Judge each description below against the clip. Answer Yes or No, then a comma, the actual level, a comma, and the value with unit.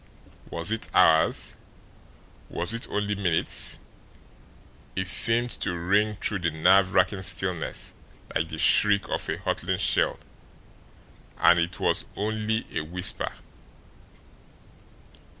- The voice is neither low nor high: No, very low, 95 Hz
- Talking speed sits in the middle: No, slow, 115 wpm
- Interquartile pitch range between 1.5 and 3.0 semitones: No, average, 3.6 semitones